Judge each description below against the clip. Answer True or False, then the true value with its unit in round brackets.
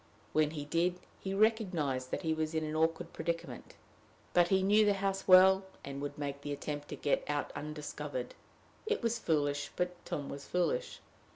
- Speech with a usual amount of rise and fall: True (4.6 semitones)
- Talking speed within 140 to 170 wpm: False (180 wpm)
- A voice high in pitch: False (165 Hz)